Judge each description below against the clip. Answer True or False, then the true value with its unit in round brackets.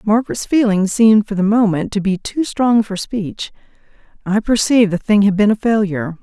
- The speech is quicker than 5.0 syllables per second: True (5.4 syllables/s)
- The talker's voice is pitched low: False (210 Hz)